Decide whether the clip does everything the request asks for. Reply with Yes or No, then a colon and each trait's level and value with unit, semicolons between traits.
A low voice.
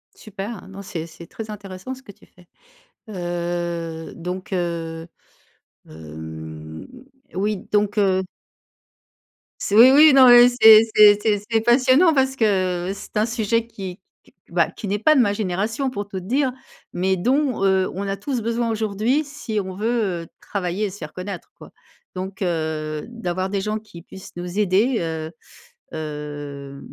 No: high, 195 Hz